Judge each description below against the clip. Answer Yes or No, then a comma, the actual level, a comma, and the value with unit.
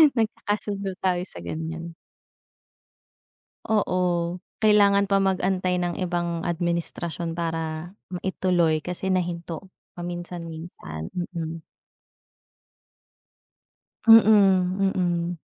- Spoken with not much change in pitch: Yes, narrow, 2.2 semitones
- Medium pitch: Yes, medium, 175 Hz